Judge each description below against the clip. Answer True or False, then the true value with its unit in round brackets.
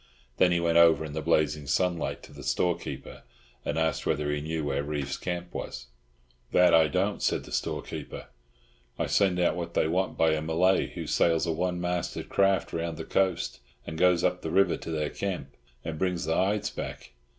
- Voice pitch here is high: False (85 Hz)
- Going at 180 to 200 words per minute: True (195 wpm)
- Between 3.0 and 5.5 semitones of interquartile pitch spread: False (2.4 semitones)